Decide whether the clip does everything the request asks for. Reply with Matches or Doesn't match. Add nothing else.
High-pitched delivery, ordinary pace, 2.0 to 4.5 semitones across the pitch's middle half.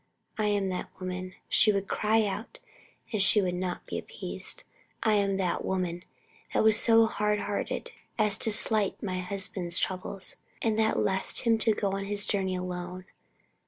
Matches